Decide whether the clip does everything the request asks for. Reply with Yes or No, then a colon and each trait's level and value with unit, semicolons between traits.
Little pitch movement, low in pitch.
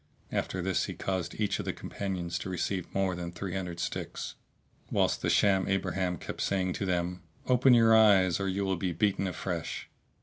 Yes: narrow, 1.7 semitones; very low, 95 Hz